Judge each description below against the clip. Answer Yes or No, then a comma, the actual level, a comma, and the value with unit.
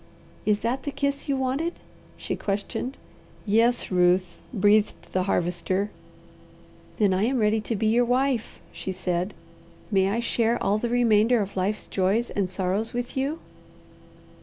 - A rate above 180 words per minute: No, average, 150 wpm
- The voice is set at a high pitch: Yes, high, 215 Hz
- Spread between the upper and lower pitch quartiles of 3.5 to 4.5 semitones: Yes, average, 4.1 semitones